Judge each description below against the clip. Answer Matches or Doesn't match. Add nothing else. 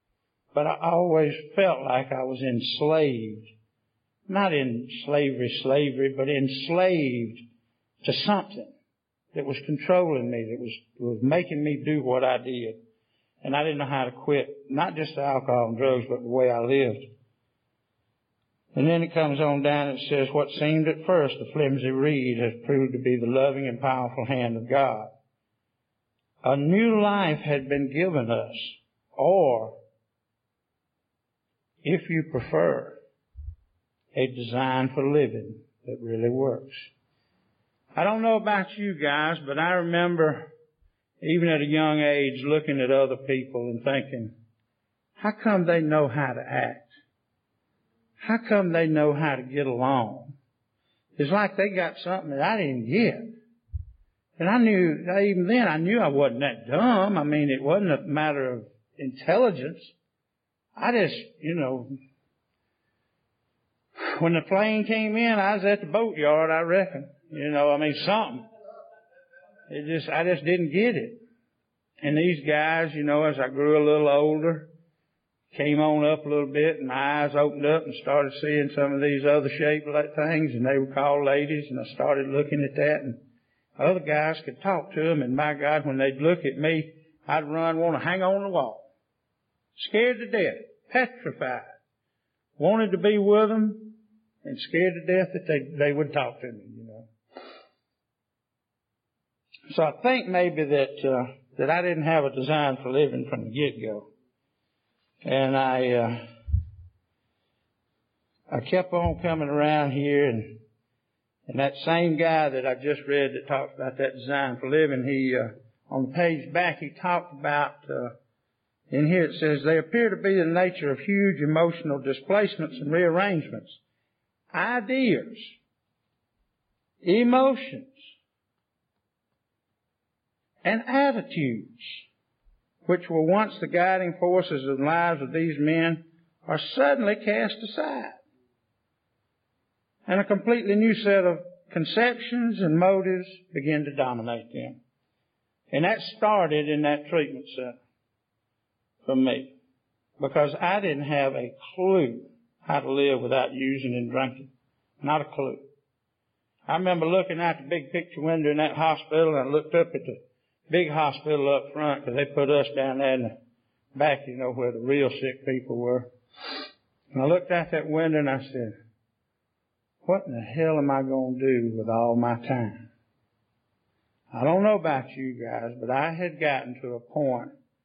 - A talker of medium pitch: Matches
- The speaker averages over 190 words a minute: Doesn't match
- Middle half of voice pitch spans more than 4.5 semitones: Matches